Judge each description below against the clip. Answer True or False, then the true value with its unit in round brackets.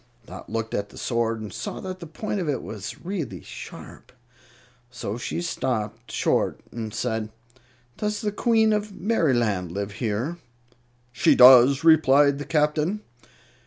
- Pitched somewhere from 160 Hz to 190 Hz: False (130 Hz)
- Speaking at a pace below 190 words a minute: True (145 wpm)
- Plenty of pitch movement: True (7.5 semitones)